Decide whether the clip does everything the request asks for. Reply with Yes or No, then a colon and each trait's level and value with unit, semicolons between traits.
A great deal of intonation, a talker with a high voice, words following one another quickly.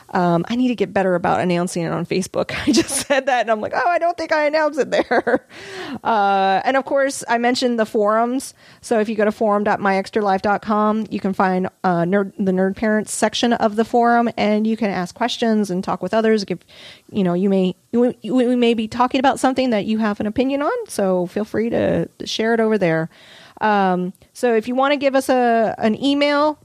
No: average, 4.4 semitones; high, 220 Hz; fast, 220 wpm